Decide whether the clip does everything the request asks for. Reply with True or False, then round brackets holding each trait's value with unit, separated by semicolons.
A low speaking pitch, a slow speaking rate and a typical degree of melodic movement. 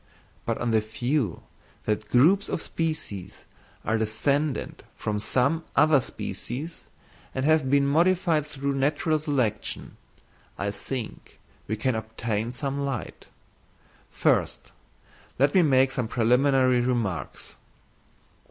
True (130 Hz; 115 wpm; 4.7 semitones)